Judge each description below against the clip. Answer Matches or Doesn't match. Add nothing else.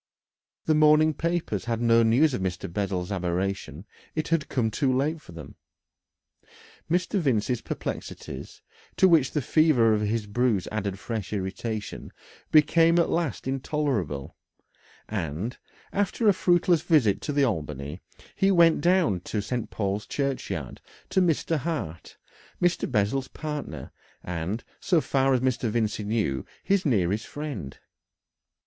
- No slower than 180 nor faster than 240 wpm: Doesn't match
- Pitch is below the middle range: Matches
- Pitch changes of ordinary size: Doesn't match